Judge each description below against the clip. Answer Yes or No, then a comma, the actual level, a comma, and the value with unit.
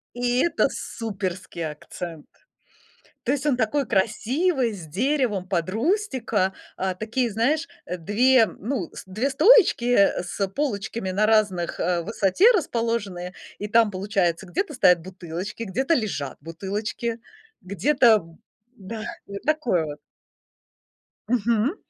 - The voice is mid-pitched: No, high, 215 Hz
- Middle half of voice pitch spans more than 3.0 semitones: Yes, average, 5.1 semitones